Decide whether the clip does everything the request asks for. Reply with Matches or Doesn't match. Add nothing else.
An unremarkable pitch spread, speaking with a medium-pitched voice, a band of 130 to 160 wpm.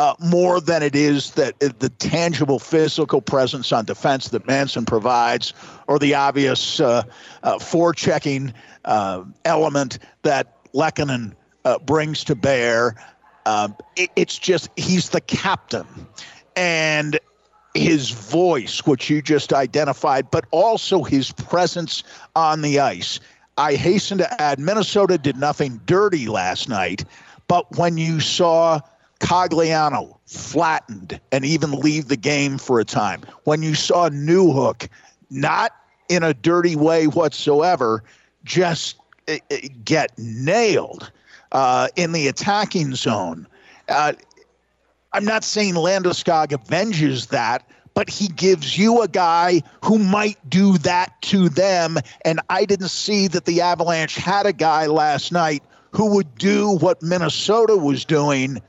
Matches